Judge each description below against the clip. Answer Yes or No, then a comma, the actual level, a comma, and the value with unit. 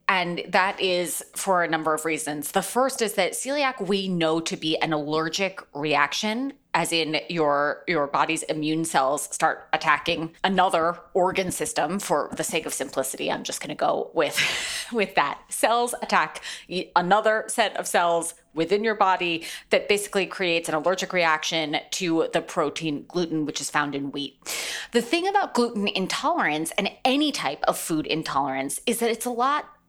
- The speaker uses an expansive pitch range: No, average, 4.3 semitones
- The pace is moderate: Yes, average, 170 wpm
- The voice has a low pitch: No, medium, 175 Hz